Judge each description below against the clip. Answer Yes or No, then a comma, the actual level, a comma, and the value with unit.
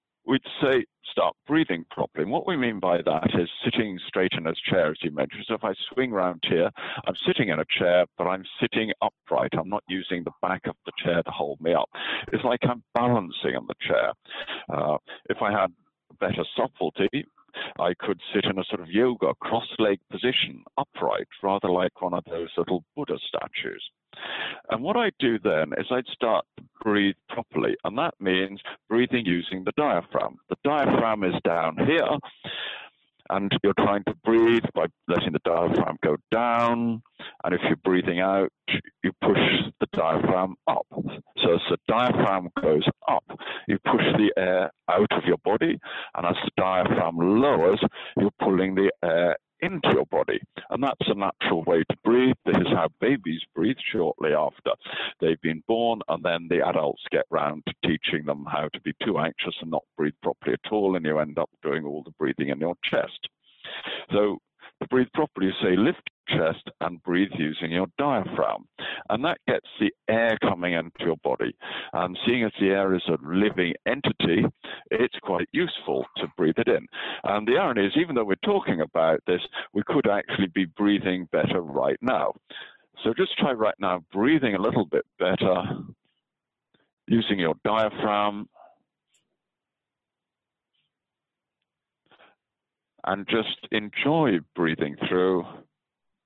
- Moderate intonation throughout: Yes, average, 4.1 semitones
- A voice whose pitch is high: No, very low, 95 Hz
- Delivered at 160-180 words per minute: Yes, average, 170 wpm